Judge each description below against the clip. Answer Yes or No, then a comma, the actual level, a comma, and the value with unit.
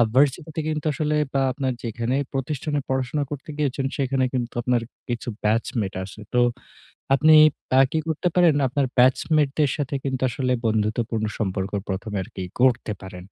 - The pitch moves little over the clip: No, average, 4.2 semitones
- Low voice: Yes, low, 130 Hz